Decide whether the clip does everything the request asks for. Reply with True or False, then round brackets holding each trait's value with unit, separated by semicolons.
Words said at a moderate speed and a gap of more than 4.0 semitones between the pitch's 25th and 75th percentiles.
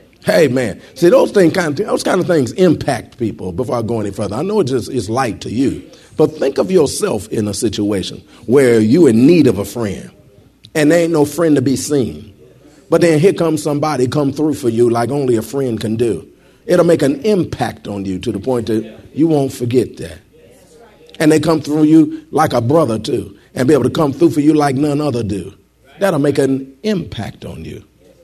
False (220 wpm; 5.4 semitones)